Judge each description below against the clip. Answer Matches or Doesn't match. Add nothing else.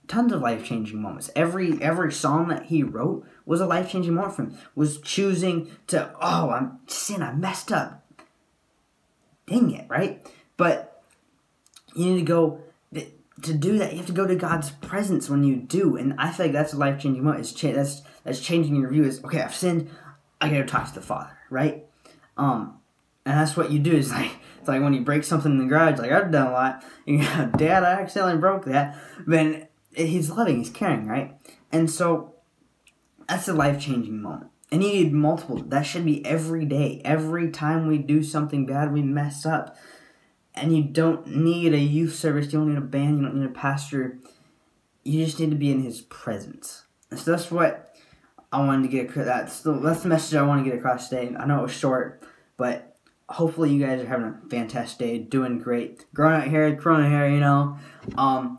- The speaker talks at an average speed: Doesn't match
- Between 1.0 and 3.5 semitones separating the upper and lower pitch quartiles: Matches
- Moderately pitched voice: Matches